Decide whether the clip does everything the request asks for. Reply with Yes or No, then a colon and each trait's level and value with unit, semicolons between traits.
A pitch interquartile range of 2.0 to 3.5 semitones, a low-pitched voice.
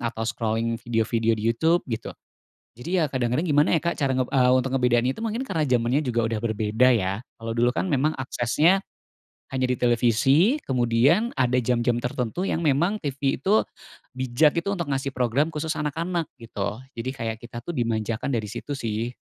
No: average, 4.4 semitones; low, 125 Hz